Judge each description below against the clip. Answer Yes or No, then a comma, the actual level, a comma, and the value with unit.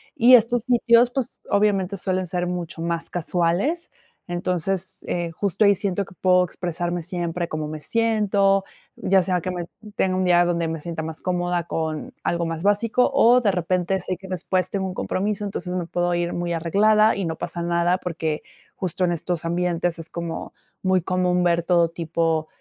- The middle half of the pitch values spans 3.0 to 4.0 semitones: No, narrow, 2.4 semitones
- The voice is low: No, medium, 180 Hz